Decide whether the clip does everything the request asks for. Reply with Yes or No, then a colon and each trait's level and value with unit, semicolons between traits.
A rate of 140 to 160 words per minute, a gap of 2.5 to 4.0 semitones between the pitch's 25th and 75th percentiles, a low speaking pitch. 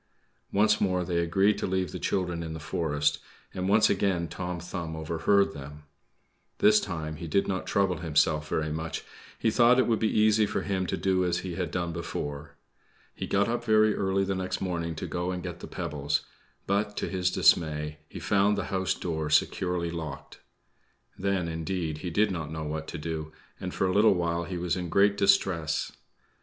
No: average, 195 wpm; average, 3.5 semitones; very low, 90 Hz